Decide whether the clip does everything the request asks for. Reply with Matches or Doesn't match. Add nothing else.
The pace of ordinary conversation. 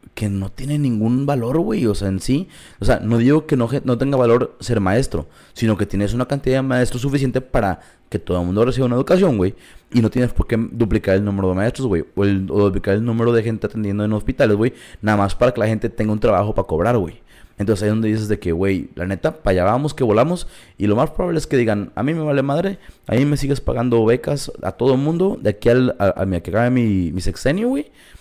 Doesn't match